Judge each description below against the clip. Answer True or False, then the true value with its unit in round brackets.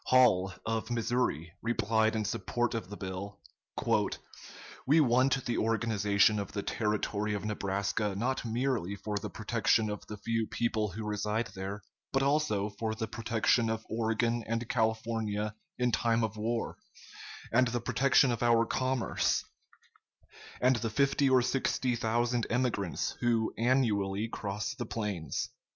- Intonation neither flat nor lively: False (2.3 semitones)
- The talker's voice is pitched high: False (115 Hz)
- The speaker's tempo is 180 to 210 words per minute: False (140 wpm)